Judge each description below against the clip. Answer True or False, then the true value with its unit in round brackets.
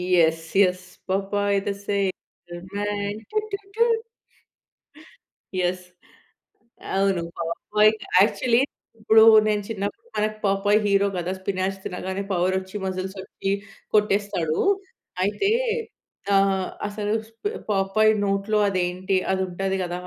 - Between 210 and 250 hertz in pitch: False (195 Hz)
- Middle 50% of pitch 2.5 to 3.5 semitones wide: False (1.8 semitones)